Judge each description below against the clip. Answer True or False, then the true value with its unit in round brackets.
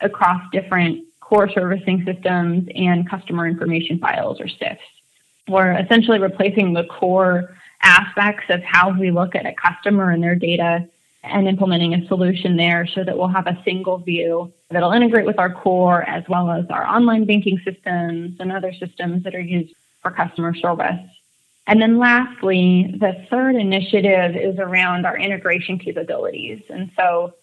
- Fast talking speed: False (160 wpm)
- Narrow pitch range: True (1.9 semitones)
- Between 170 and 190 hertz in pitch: True (185 Hz)